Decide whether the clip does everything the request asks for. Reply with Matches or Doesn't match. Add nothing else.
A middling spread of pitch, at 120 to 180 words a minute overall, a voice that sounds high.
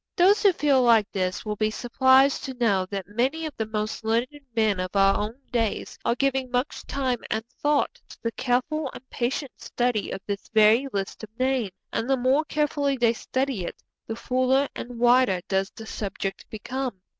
Doesn't match